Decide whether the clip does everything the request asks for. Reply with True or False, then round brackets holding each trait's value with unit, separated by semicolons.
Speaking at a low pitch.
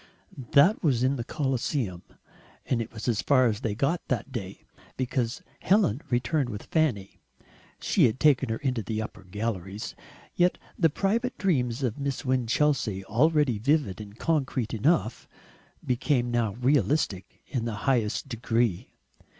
True (125 Hz)